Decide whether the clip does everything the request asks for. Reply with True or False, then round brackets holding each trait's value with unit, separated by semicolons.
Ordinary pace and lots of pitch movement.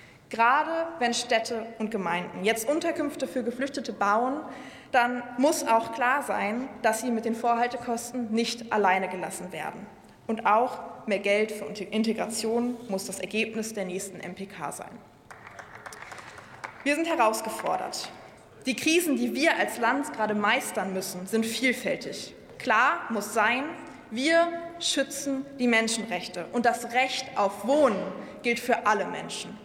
False (135 wpm; 3.5 semitones)